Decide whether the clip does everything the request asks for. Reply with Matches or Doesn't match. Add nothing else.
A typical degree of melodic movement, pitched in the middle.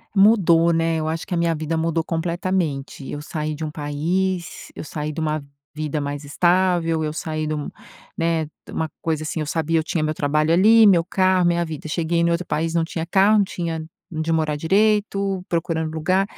Doesn't match